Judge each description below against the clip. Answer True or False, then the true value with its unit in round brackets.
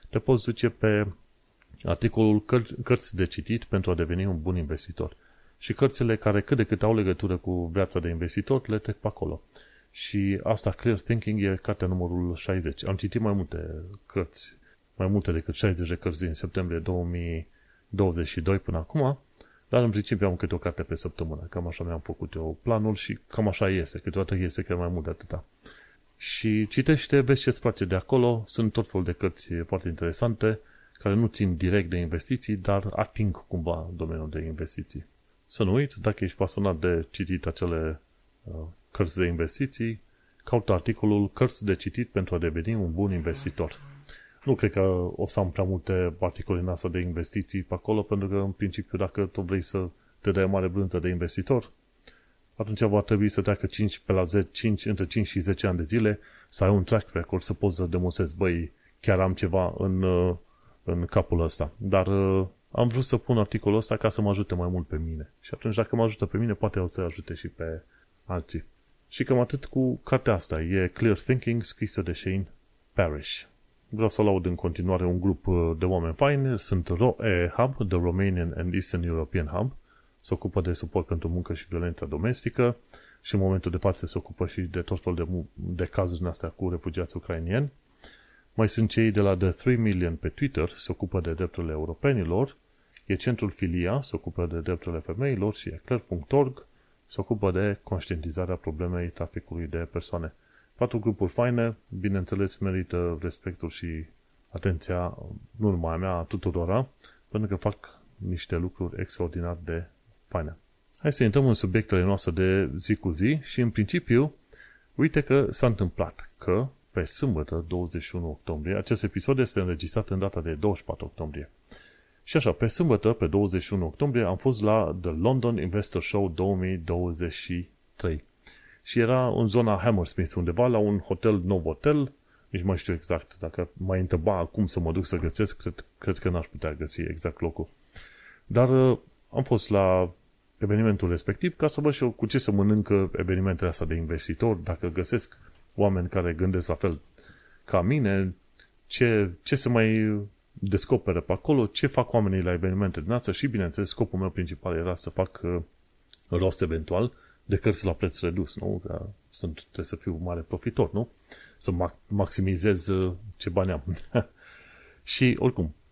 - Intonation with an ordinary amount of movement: True (3.7 semitones)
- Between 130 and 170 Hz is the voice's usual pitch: False (95 Hz)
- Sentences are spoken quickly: True (180 wpm)